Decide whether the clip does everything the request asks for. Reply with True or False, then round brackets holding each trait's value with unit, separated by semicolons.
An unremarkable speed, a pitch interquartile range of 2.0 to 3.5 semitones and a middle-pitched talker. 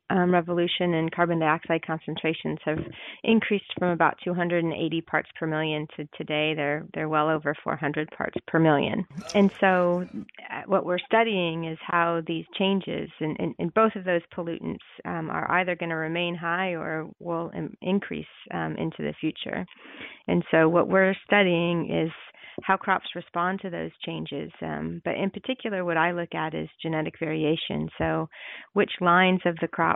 True (170 wpm; 2.7 semitones; 170 Hz)